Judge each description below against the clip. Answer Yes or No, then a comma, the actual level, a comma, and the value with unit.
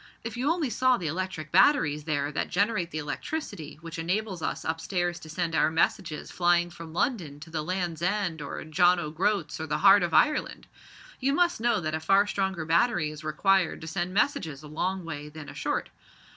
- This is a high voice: No, medium, 175 Hz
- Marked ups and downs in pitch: No, average, 4.0 semitones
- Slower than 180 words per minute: No, fast, 205 wpm